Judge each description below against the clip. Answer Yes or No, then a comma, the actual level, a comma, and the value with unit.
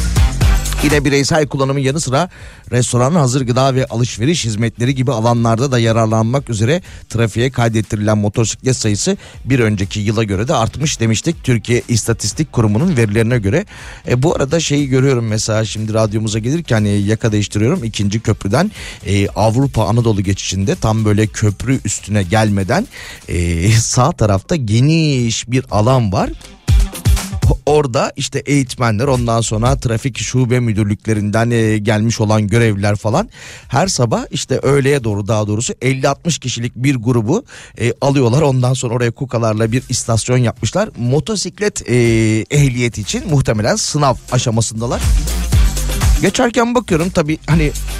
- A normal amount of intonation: Yes, average, 3.9 semitones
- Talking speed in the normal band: Yes, average, 130 wpm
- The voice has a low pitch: Yes, low, 115 Hz